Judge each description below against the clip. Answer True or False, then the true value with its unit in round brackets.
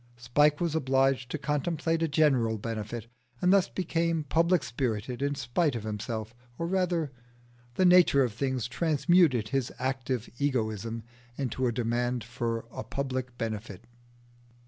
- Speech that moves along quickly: False (140 wpm)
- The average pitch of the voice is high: False (130 Hz)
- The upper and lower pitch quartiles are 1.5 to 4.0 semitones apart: False (5.1 semitones)